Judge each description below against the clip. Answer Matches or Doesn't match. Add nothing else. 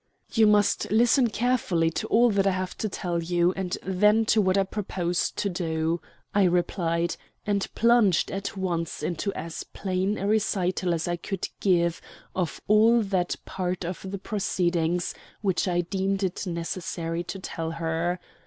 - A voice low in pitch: Doesn't match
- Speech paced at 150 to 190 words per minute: Matches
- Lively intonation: Doesn't match